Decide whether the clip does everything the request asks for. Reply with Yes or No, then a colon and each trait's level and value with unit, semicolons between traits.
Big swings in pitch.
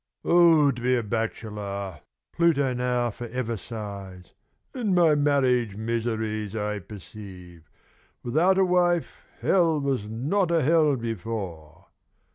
Yes: wide, 6.4 semitones